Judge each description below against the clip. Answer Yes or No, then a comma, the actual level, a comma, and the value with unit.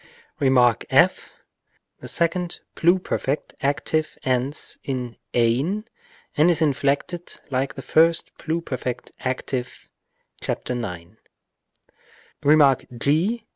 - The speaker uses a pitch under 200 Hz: Yes, medium, 140 Hz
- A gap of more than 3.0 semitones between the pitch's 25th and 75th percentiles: Yes, average, 4.5 semitones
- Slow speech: Yes, slow, 95 wpm